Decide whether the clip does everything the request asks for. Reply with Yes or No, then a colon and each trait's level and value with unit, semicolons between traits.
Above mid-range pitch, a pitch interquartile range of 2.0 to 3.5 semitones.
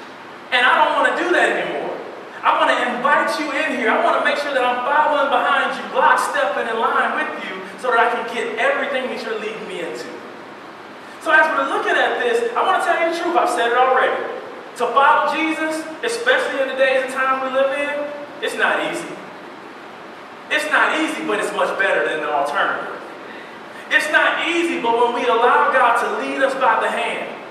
No: very high, 290 Hz; average, 4.1 semitones